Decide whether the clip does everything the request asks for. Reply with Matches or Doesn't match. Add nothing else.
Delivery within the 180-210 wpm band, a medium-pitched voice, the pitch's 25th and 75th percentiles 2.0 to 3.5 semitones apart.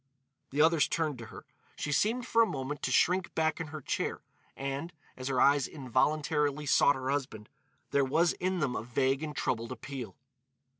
Matches